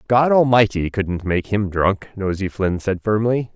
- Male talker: Yes, male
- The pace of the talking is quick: No, average, 170 wpm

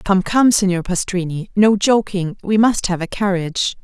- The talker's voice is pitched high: Yes, high, 195 Hz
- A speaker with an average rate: Yes, average, 170 wpm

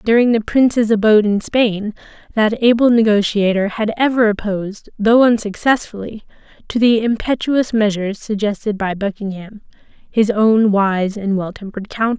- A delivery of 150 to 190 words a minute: No, average, 140 wpm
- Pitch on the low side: No, high, 215 Hz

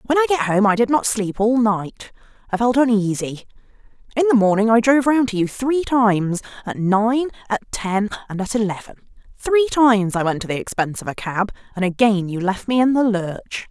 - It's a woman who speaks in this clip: Yes, female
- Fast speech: Yes, fast, 210 wpm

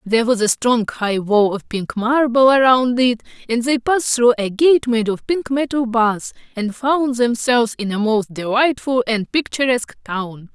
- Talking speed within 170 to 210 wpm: Yes, average, 180 wpm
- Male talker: No, female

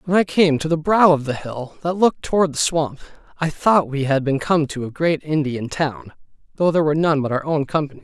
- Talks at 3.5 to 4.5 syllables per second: Yes, 4.4 syllables/s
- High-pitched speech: No, medium, 155 Hz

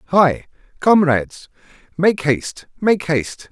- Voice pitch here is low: No, medium, 160 Hz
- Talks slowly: Yes, slow, 100 wpm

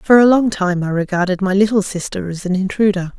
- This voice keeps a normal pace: No, fast, 225 wpm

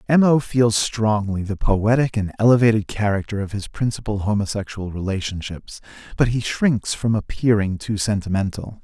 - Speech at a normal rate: Yes, average, 145 wpm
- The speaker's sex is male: Yes, male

